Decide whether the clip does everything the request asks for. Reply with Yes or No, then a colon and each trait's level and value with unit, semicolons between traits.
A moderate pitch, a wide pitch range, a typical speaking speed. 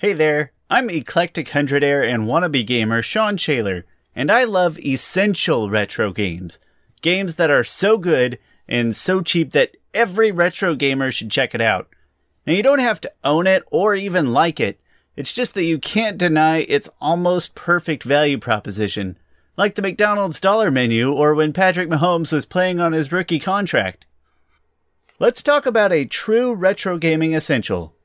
Yes: medium, 160 Hz; wide, 6.7 semitones; average, 165 wpm